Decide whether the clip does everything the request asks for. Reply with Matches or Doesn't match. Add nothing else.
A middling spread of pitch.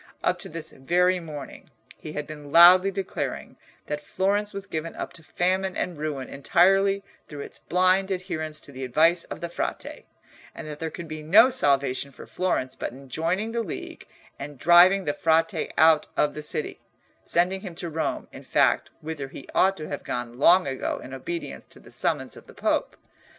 Matches